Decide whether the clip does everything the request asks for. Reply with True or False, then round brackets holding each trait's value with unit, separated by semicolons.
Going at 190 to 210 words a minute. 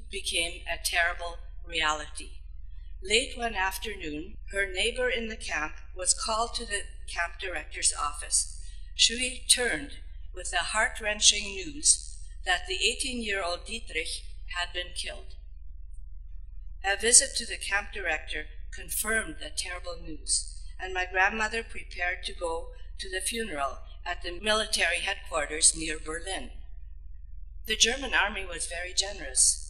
False (135 wpm)